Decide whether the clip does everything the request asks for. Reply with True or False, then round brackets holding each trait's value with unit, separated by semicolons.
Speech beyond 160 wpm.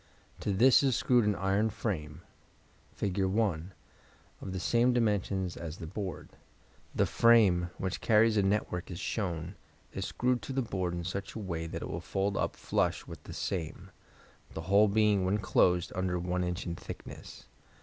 True (175 wpm)